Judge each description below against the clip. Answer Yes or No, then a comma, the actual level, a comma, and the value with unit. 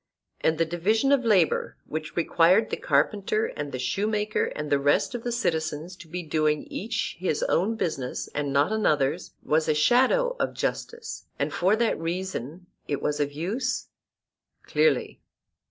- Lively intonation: Yes, wide, 6.4 semitones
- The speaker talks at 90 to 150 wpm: No, average, 160 wpm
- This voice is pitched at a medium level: Yes, medium, 170 Hz